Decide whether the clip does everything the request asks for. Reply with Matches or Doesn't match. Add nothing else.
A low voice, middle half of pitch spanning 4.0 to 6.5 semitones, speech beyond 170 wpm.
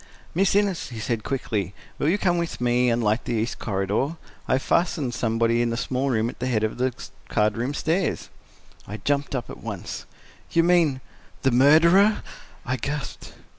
Matches